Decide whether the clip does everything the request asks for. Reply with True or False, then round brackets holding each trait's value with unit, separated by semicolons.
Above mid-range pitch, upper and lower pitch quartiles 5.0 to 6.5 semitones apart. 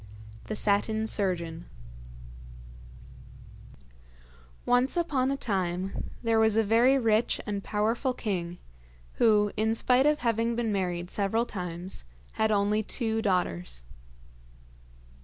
False (215 Hz; 3.4 semitones)